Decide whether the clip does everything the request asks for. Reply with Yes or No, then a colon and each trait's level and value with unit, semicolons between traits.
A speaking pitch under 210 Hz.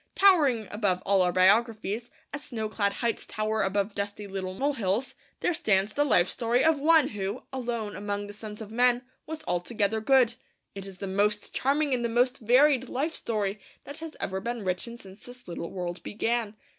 No: high, 220 Hz